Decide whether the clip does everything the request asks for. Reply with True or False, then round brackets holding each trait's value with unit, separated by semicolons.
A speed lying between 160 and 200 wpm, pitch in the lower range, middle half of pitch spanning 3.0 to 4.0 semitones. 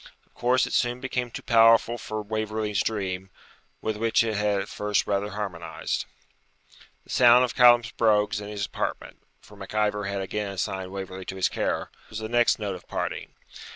False (185 wpm; 105 Hz; 2.5 semitones)